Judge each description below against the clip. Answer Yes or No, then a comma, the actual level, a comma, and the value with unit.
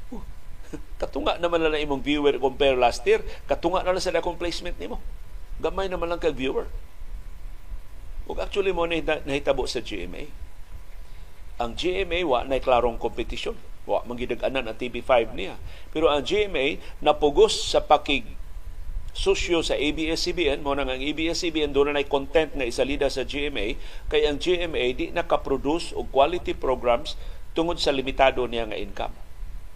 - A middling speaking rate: Yes, average, 145 wpm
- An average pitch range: No, wide, 6.0 semitones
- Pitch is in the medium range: Yes, medium, 145 Hz